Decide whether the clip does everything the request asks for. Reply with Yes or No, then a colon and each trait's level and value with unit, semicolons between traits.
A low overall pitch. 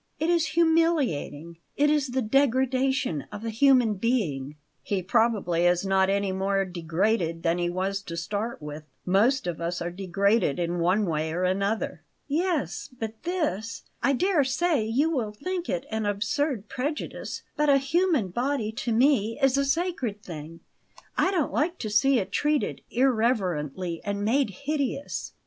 No: high, 220 Hz